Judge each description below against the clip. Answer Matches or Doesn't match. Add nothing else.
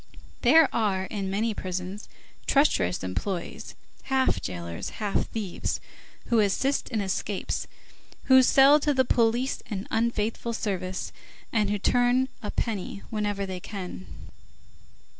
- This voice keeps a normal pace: Doesn't match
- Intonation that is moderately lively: Matches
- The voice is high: Matches